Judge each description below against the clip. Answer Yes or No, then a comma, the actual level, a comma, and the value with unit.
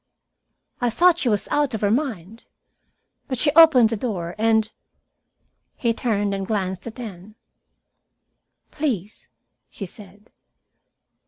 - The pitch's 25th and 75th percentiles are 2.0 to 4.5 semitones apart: Yes, average, 3.9 semitones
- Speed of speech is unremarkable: No, slow, 130 wpm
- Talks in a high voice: Yes, high, 220 Hz